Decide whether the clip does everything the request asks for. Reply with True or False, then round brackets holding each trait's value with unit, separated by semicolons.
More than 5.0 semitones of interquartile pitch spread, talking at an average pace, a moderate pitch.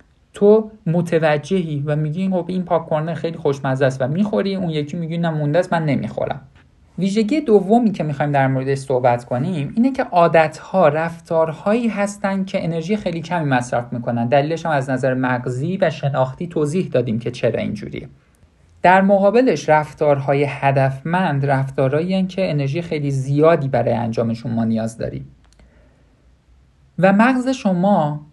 True (5.6 semitones; 140 wpm; 155 Hz)